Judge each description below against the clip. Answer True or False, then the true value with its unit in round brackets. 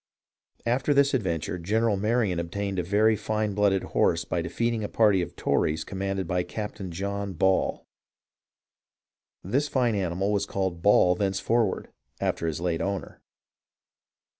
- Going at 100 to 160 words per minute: True (140 wpm)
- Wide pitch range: False (3.2 semitones)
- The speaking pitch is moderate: False (100 Hz)